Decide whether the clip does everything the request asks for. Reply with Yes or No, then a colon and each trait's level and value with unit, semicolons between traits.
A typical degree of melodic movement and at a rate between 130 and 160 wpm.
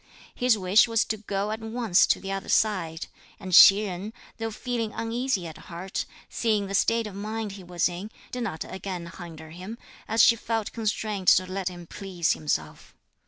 No: average, 3.7 semitones; average, 185 wpm